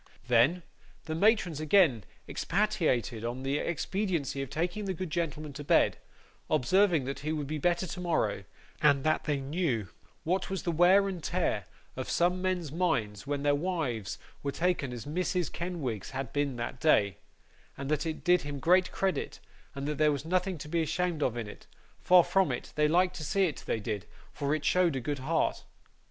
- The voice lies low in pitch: No, medium, 155 Hz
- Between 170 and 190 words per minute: Yes, average, 185 wpm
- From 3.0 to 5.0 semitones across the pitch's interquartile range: Yes, average, 4.5 semitones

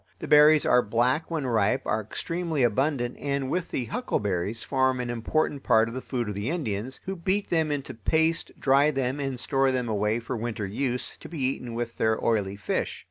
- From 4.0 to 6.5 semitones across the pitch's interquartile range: Yes, average, 4.5 semitones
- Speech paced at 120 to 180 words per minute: No, average, 200 wpm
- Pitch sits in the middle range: No, low, 130 Hz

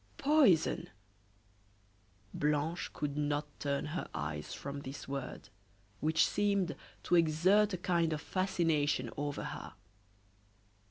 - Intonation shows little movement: No, average, 3.8 semitones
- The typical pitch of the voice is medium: Yes, medium, 155 Hz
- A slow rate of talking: Yes, slow, 110 wpm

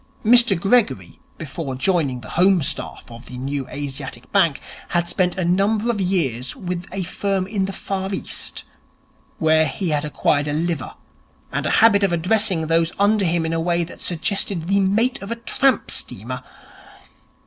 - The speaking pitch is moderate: Yes, medium, 175 Hz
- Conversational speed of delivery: Yes, average, 170 wpm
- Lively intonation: No, average, 4.2 semitones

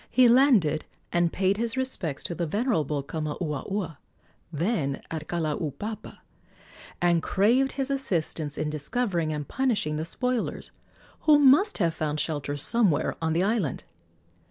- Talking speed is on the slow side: Yes, slow, 130 wpm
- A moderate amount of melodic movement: No, wide, 7.4 semitones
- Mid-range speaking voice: Yes, medium, 170 Hz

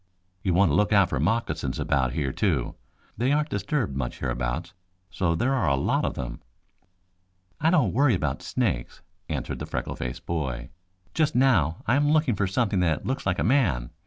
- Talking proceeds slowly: No, average, 190 wpm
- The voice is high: No, very low, 95 Hz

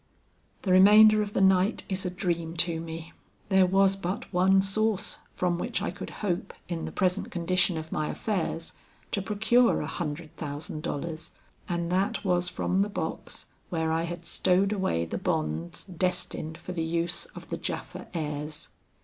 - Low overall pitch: No, medium, 180 Hz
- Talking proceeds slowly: No, average, 170 wpm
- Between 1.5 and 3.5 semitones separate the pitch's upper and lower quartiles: Yes, average, 2.9 semitones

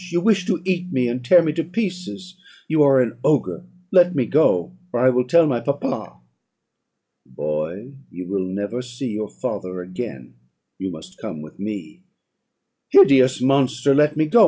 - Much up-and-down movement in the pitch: Yes, wide, 8.5 semitones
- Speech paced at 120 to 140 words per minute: No, average, 170 wpm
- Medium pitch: No, low, 130 Hz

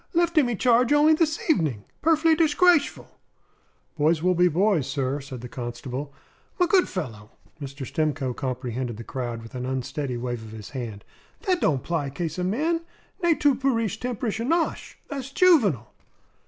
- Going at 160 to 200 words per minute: Yes, average, 165 wpm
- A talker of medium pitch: Yes, medium, 165 Hz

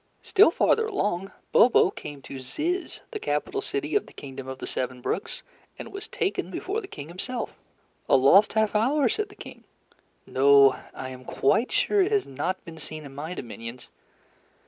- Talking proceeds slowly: No, average, 180 wpm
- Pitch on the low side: No, high, 190 Hz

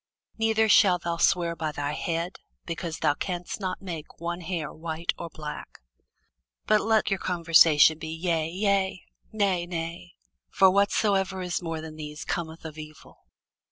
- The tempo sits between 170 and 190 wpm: No, average, 155 wpm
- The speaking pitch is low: No, medium, 170 Hz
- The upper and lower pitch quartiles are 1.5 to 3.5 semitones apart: Yes, average, 2.8 semitones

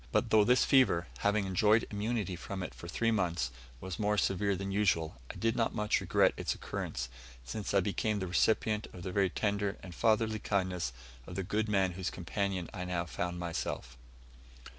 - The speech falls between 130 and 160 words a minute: No, average, 185 wpm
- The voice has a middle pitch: No, low, 100 Hz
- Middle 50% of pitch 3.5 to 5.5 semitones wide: No, average, 3.1 semitones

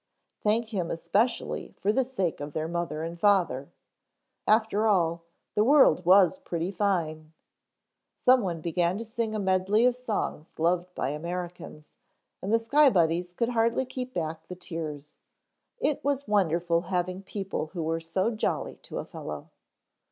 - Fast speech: No, average, 150 wpm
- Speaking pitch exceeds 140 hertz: Yes, medium, 185 Hz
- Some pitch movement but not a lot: Yes, average, 4.9 semitones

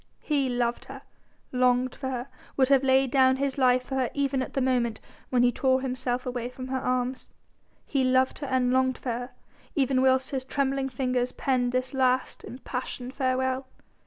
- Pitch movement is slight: Yes, narrow, 0.9 semitones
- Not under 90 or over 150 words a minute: No, average, 185 wpm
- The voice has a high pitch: Yes, very high, 260 Hz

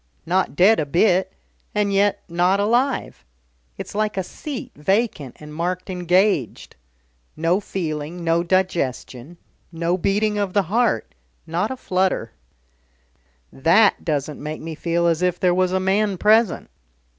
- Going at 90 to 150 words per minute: Yes, average, 140 wpm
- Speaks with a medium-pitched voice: Yes, medium, 180 Hz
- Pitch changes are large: No, average, 3.5 semitones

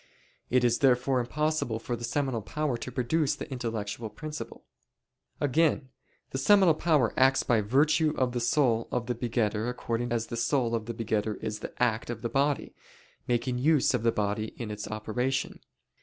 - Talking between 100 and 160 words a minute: No, average, 175 wpm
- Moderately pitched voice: No, low, 120 Hz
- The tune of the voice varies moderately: Yes, average, 3.2 semitones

